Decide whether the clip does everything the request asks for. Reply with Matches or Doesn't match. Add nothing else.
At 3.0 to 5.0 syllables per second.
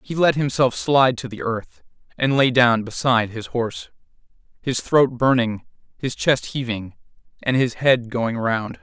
Matches